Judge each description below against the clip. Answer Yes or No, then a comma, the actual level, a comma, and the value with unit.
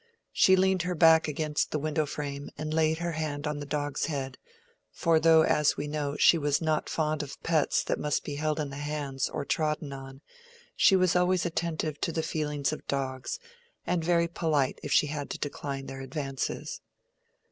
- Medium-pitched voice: Yes, medium, 150 Hz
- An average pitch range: No, narrow, 2.2 semitones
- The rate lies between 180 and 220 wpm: Yes, average, 190 wpm